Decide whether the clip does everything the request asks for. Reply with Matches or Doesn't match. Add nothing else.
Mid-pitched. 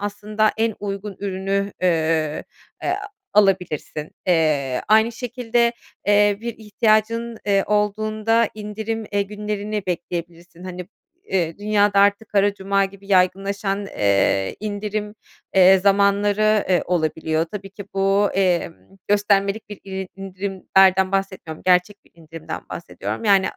Doesn't match